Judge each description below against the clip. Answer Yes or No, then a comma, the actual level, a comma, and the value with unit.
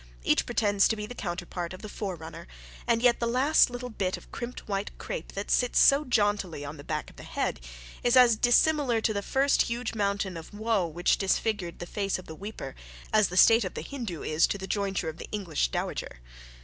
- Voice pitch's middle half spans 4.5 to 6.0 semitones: Yes, average, 4.9 semitones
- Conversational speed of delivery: No, fast, 215 wpm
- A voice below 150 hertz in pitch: No, high, 205 Hz